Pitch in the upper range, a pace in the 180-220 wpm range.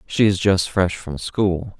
No: very low, 90 Hz; average, 200 wpm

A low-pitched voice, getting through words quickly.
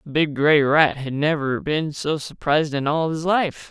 No: medium, 150 Hz; fast, 210 wpm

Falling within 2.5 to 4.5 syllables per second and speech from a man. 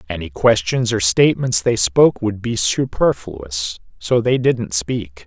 Yes: 4.1 syllables/s; male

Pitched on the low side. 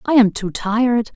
No: high, 225 Hz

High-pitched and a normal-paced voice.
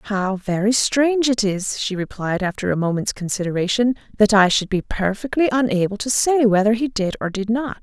Yes: high, 215 Hz; average, 190 wpm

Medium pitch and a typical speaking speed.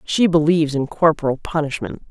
Yes: medium, 150 Hz; average, 145 wpm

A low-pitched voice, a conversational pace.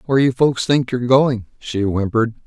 Yes: low, 125 Hz; average, 195 wpm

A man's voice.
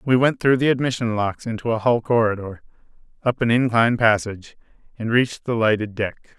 Yes: male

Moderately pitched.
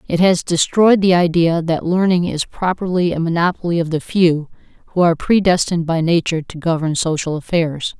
Yes: medium, 170 Hz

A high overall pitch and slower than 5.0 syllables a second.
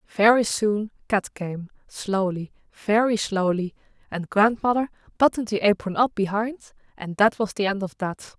Yes: high, 205 Hz; 4.8 syllables/s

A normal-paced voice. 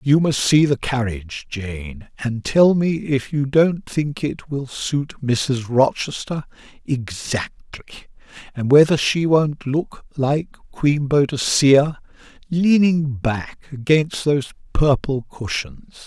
No: slow, 125 wpm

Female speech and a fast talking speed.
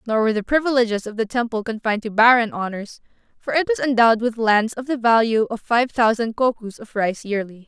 Yes: female; fast, 210 wpm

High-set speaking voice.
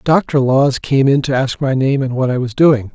No: low, 135 Hz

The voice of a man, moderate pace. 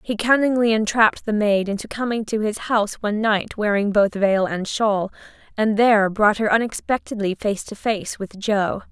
No: female; average, 180 wpm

